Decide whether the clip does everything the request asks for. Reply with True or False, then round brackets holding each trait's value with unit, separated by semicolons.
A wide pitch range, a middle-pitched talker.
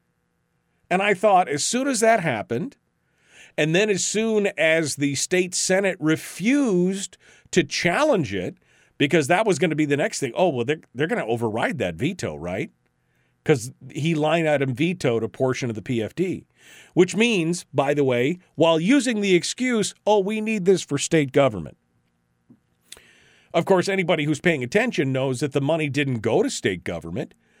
True (5.9 semitones; 160 Hz)